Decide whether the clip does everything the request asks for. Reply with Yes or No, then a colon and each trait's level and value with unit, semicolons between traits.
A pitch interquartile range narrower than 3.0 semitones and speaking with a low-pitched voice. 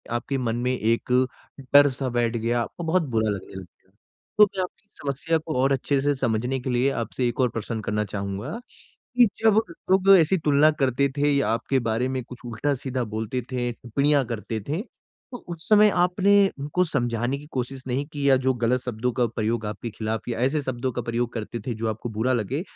No: average, 3.9 semitones; low, 125 Hz